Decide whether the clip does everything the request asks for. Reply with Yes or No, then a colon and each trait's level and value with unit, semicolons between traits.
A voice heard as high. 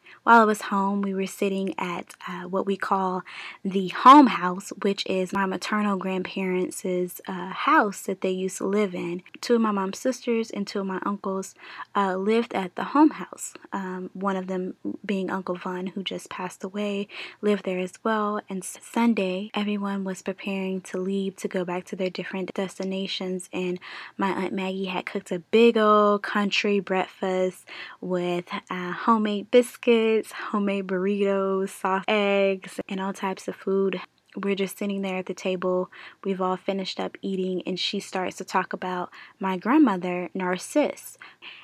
Yes: high, 195 Hz